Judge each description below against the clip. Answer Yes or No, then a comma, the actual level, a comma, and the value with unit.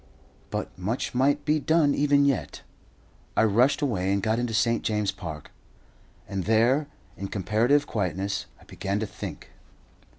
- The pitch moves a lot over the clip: Yes, wide, 6.1 semitones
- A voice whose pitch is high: No, low, 110 Hz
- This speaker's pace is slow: No, average, 145 wpm